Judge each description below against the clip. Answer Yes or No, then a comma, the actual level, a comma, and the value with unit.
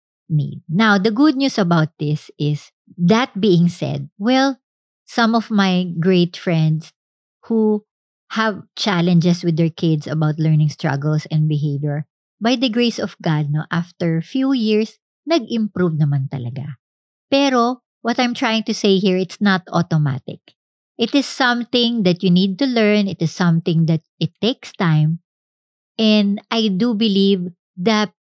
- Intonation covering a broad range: Yes, wide, 5.8 semitones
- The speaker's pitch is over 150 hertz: Yes, high, 190 Hz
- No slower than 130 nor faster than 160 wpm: Yes, average, 155 wpm